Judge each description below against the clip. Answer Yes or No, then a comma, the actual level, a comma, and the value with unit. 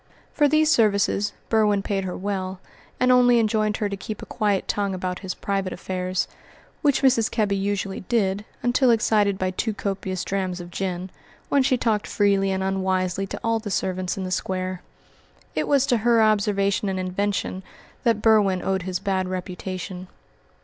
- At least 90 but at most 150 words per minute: No, average, 170 wpm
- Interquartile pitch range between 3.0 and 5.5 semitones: No, narrow, 2.6 semitones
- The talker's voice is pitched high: Yes, high, 195 Hz